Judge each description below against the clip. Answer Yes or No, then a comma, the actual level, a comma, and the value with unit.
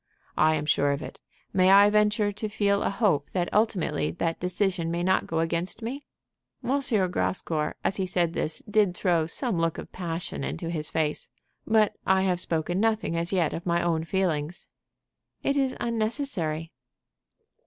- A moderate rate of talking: Yes, average, 170 wpm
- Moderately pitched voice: Yes, medium, 180 Hz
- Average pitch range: Yes, average, 4.2 semitones